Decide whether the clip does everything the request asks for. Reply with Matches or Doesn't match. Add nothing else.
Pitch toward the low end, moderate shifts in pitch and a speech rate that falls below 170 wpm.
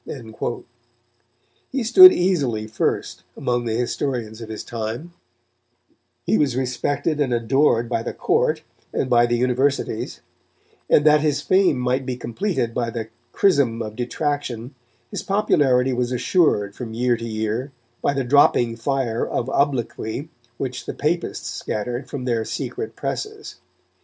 Matches